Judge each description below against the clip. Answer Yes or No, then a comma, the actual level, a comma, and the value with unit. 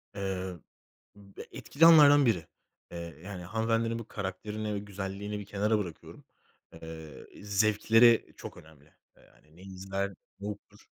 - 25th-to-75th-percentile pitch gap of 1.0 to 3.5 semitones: Yes, average, 2.7 semitones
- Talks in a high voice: No, low, 100 Hz